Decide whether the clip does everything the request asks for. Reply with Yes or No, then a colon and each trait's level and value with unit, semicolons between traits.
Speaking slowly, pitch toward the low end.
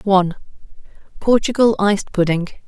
No: slow, 65 wpm; high, 200 Hz